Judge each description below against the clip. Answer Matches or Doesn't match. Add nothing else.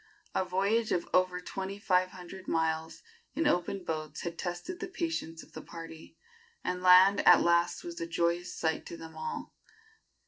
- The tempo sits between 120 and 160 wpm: Doesn't match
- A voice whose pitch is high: Doesn't match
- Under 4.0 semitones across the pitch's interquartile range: Matches